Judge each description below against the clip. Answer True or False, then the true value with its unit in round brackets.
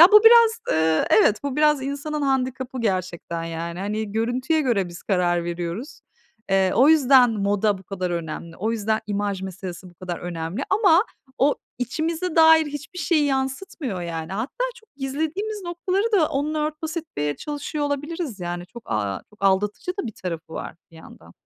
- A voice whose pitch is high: True (235 Hz)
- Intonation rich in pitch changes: True (8.9 semitones)